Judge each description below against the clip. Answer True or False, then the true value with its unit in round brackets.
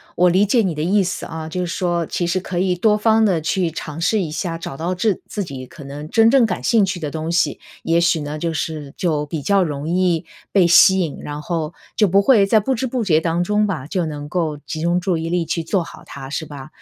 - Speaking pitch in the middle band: True (170 Hz)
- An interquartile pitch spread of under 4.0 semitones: True (3.5 semitones)